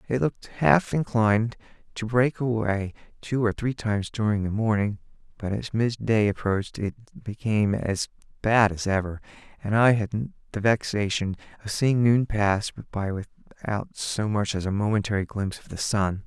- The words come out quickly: No, average, 165 wpm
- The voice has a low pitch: Yes, low, 110 Hz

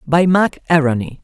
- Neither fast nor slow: Yes, average, 145 wpm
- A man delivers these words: Yes, male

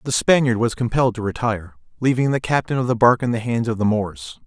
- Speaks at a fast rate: Yes, fast, 240 wpm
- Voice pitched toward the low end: Yes, low, 120 Hz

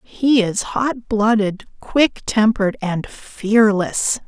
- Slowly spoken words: Yes, slow, 110 wpm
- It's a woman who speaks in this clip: Yes, female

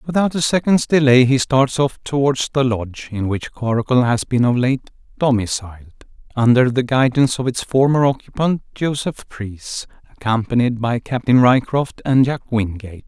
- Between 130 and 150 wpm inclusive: Yes, average, 145 wpm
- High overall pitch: No, low, 125 Hz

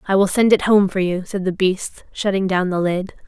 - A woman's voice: Yes, female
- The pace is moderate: No, fast, 255 wpm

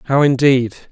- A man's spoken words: Yes, male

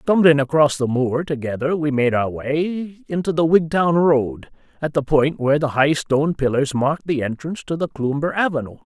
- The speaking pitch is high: No, medium, 150 Hz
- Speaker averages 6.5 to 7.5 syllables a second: No, 5.1 syllables/s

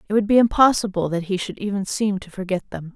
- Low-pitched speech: No, high, 200 Hz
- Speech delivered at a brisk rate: Yes, fast, 245 wpm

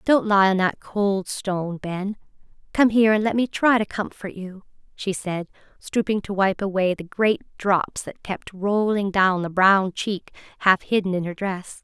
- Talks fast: No, average, 190 wpm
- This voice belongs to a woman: Yes, female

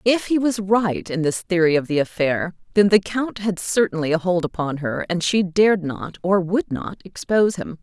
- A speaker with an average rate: No, fast, 215 wpm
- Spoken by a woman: Yes, female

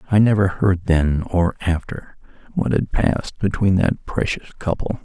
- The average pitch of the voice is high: No, very low, 95 Hz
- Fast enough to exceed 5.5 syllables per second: No, 4.4 syllables/s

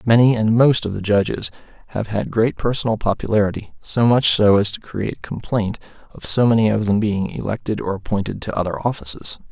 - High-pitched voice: No, low, 105 Hz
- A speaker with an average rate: Yes, average, 185 wpm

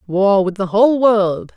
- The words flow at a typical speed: Yes, average, 190 wpm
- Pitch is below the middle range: No, high, 205 Hz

